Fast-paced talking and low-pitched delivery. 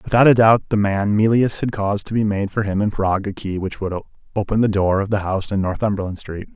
Yes: fast, 255 wpm; low, 100 Hz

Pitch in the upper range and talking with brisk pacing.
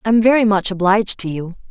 Yes: high, 205 Hz; fast, 210 wpm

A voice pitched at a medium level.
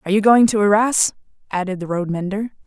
No: high, 200 Hz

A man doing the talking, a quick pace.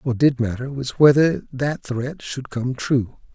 No: male; average, 180 wpm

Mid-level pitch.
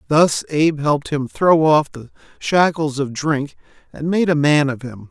Yes: medium, 150 Hz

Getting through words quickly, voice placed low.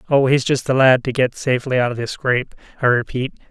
Yes: fast, 240 wpm; low, 130 Hz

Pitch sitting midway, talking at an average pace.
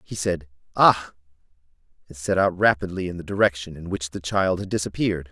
No: very low, 90 Hz; average, 180 wpm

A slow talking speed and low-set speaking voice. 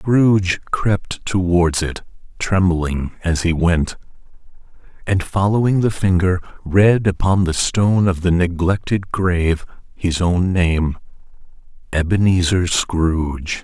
Yes: slow, 110 wpm; very low, 90 Hz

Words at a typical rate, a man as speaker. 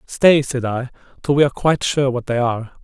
No: fast, 235 wpm; male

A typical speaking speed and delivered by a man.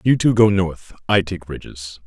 Yes: average, 175 wpm; male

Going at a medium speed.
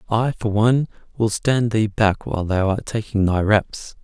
Yes: average, 195 wpm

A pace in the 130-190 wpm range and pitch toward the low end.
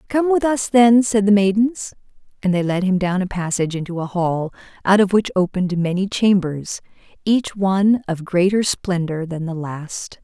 No: average, 180 wpm; high, 190 Hz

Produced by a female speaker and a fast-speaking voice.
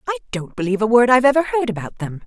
Yes: female; fast, 265 wpm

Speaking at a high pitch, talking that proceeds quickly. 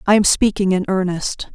No: high, 195 Hz; average, 195 wpm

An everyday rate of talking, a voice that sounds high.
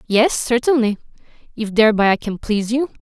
Yes: average, 160 wpm; high, 230 Hz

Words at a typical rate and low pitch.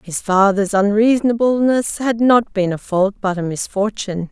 No: average, 155 wpm; high, 210 Hz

